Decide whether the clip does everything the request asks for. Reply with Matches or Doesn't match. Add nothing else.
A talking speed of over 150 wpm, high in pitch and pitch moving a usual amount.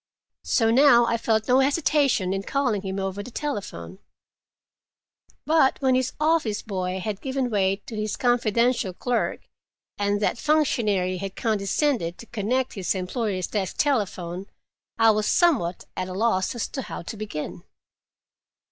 Doesn't match